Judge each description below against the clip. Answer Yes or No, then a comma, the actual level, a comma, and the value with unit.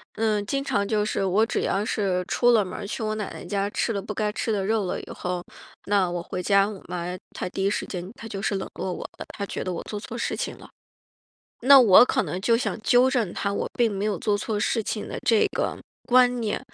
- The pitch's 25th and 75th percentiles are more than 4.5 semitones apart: No, narrow, 2.6 semitones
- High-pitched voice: Yes, high, 205 Hz